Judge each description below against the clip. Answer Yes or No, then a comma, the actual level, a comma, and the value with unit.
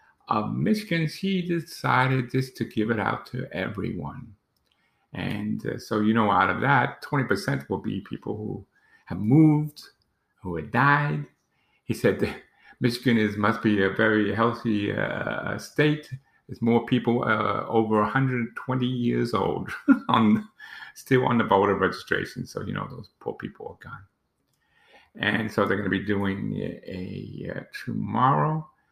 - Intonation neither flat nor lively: Yes, average, 5.0 semitones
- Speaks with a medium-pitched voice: No, low, 120 Hz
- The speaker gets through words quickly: No, average, 155 wpm